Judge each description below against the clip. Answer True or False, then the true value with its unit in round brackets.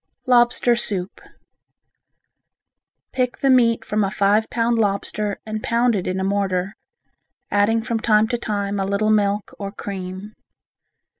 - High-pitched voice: True (210 Hz)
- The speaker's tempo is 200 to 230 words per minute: False (140 wpm)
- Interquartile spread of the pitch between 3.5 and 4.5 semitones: False (2.6 semitones)